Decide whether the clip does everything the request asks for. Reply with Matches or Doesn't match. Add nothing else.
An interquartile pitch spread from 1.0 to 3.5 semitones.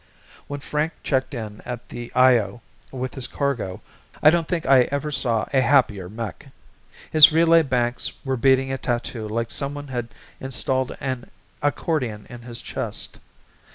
Matches